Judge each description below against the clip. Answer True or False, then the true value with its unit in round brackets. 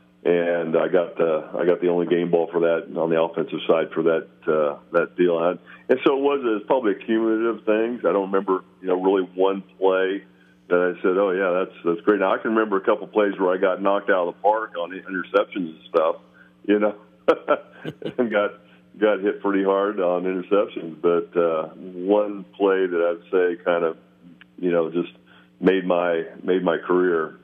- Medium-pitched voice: False (90 Hz)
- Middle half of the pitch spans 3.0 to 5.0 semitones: False (2.6 semitones)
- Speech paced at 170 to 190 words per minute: False (205 wpm)